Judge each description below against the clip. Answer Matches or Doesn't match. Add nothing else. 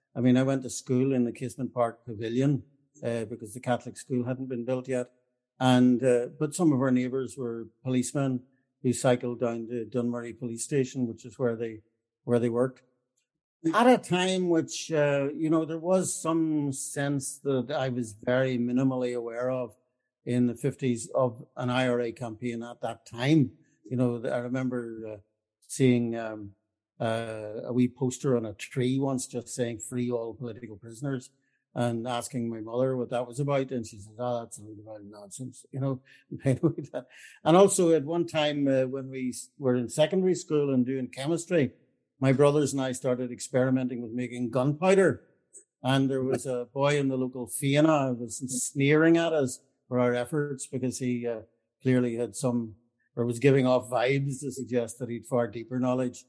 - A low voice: Matches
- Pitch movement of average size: Doesn't match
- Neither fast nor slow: Matches